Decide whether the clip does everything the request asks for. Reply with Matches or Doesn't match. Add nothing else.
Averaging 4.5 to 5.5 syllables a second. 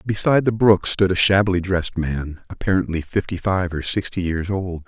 Matches